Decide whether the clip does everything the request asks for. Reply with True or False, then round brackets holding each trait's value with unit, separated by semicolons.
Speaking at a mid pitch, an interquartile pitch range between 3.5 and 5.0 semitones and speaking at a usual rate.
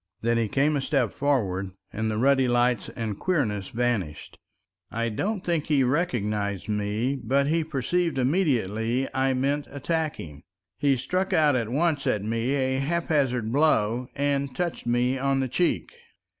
False (130 Hz; 4.3 semitones; 155 wpm)